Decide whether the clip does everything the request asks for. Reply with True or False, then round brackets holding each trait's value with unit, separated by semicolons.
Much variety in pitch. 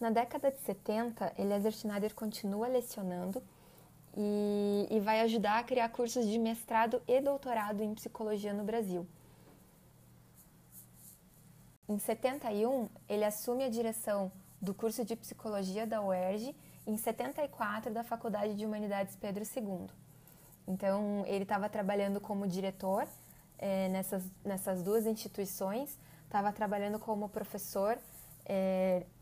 False (2.7 semitones)